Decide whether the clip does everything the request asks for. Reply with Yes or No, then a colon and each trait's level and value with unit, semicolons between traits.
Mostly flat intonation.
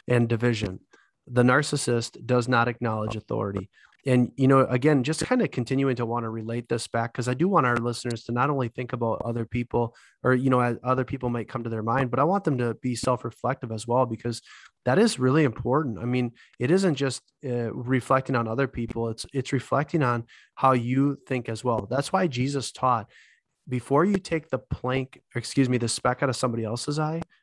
Yes: narrow, 2.3 semitones